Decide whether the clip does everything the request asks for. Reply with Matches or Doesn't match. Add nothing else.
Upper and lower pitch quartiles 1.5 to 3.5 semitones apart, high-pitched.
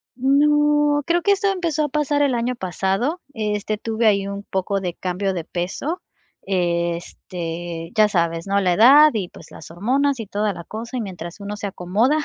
Doesn't match